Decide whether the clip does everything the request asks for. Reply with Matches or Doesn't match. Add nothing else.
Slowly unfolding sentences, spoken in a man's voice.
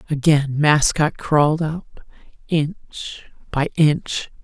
Doesn't match